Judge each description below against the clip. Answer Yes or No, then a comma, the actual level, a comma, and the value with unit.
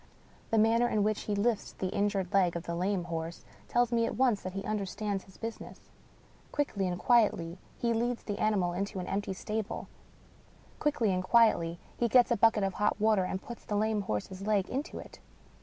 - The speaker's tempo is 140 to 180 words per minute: No, fast, 205 wpm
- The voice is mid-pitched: No, high, 205 Hz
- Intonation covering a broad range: No, average, 3.3 semitones